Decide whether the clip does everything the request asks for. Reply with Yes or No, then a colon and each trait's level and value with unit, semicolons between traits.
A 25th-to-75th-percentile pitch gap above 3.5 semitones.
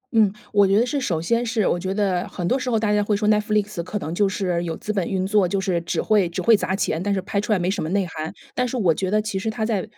No: average, 2.7 semitones